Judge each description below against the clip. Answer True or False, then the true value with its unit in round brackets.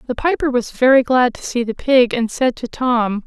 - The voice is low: False (245 Hz)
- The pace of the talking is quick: True (240 wpm)